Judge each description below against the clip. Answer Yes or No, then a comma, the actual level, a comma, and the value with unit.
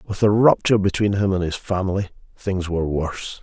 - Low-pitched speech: Yes, very low, 95 Hz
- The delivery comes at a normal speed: Yes, average, 195 wpm